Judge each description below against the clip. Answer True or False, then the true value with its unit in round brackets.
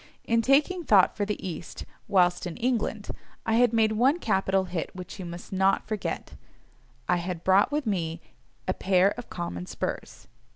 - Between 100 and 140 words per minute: False (165 wpm)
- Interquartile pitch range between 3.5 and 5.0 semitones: True (4.3 semitones)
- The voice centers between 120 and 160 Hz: False (195 Hz)